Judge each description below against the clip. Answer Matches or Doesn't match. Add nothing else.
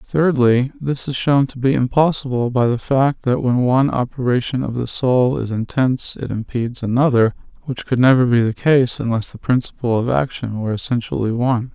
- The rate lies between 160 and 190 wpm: Matches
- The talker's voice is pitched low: Matches